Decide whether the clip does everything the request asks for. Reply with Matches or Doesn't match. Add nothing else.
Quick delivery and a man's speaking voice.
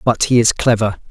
Matches